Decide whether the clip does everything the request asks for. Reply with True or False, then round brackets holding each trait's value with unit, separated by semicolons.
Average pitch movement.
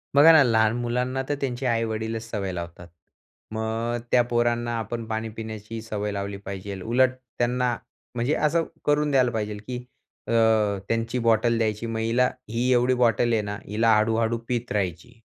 False (1.9 semitones)